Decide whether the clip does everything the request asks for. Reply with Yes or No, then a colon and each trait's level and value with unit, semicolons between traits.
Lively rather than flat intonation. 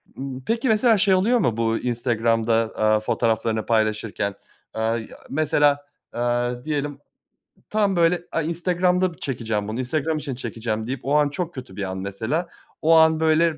Yes: wide, 6.4 semitones